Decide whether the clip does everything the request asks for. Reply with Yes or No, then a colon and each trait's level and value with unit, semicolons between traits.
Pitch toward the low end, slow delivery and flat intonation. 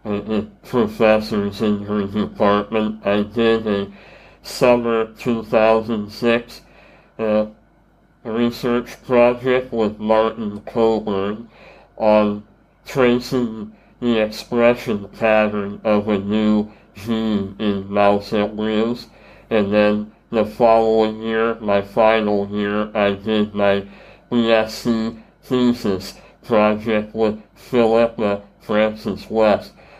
Yes: low, 110 Hz; slow, 90 wpm; narrow, 1.5 semitones